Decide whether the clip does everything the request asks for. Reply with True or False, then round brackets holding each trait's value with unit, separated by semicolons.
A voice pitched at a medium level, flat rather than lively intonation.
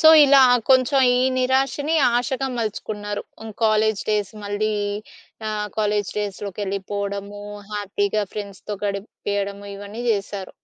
False (205 Hz; 1.6 semitones)